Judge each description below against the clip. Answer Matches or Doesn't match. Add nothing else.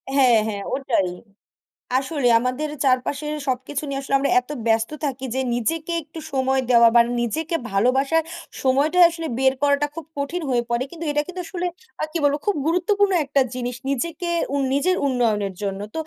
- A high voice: Matches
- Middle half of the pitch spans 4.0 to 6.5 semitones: Matches